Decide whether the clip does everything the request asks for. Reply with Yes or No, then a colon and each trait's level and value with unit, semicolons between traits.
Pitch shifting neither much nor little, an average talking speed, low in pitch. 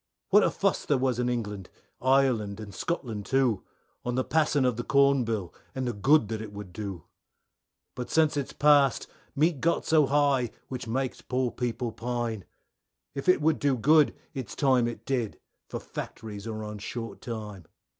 Yes: average, 4.0 semitones; average, 175 wpm; low, 125 Hz